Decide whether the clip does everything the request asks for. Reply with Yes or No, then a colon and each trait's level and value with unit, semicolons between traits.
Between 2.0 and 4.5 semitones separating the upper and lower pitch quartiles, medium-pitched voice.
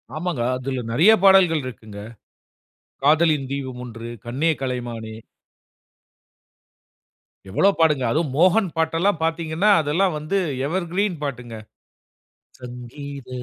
No: average, 5.3 semitones; medium, 150 Hz